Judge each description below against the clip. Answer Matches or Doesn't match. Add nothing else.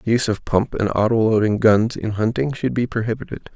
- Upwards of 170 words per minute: Matches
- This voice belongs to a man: Matches